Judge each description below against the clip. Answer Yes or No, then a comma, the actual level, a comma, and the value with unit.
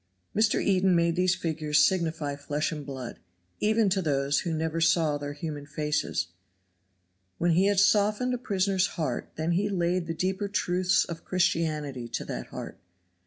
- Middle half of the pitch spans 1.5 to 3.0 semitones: No, average, 4.0 semitones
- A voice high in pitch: No, medium, 170 Hz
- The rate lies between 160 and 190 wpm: Yes, average, 165 wpm